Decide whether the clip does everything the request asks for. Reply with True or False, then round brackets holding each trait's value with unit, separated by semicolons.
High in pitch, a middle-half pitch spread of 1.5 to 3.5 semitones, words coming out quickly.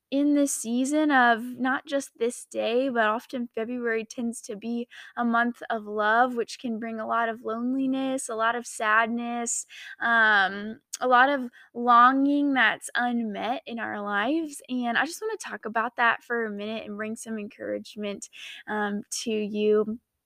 False (235 Hz; 2.7 semitones; 170 wpm)